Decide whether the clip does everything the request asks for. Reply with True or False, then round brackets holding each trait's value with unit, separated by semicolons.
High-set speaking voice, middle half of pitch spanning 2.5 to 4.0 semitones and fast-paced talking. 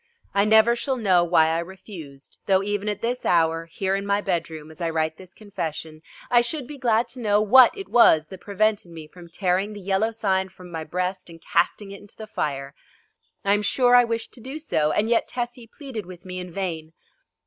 False (195 Hz; 4.8 semitones; 215 wpm)